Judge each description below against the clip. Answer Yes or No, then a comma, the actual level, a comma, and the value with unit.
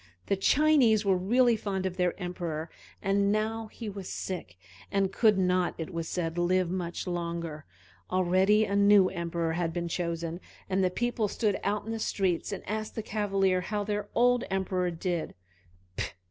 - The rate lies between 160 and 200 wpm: Yes, average, 170 wpm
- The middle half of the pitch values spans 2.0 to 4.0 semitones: Yes, average, 3.1 semitones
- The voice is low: No, high, 190 Hz